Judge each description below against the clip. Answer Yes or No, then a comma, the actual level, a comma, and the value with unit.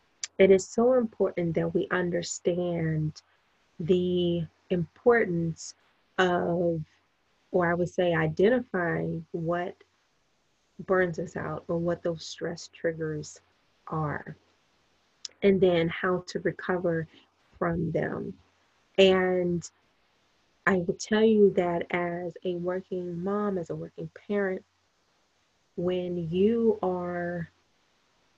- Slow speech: Yes, slow, 105 wpm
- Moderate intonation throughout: No, narrow, 1.7 semitones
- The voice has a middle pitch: Yes, medium, 180 Hz